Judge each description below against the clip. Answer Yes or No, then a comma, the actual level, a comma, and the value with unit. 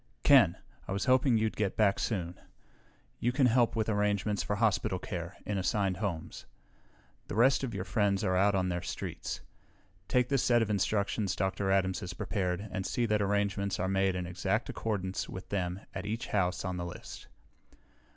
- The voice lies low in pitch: Yes, low, 100 Hz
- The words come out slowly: No, average, 180 wpm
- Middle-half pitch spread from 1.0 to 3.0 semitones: Yes, average, 2.7 semitones